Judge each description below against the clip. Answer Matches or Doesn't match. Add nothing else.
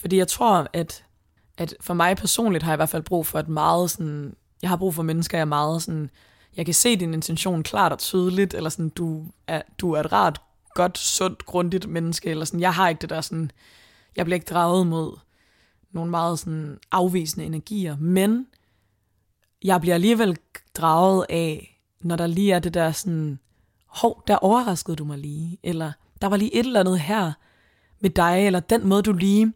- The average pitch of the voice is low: Doesn't match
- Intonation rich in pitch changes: Doesn't match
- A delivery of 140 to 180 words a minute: Doesn't match